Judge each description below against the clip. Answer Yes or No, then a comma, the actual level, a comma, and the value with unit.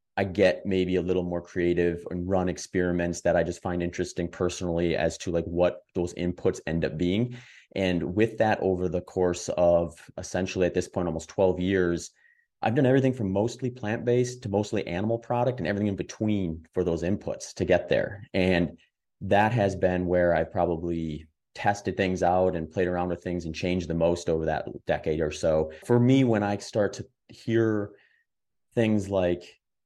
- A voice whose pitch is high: No, very low, 90 Hz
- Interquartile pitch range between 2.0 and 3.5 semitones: Yes, average, 2.9 semitones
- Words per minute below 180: No, average, 185 wpm